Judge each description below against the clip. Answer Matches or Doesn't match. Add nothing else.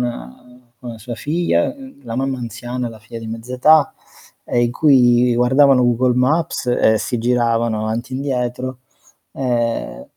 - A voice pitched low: Matches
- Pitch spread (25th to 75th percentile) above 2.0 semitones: Doesn't match